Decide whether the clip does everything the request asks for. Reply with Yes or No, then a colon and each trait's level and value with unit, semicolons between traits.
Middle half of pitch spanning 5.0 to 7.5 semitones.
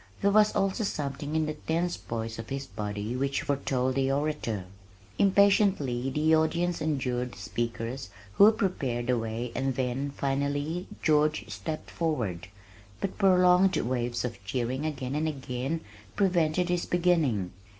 Yes: wide, 5.4 semitones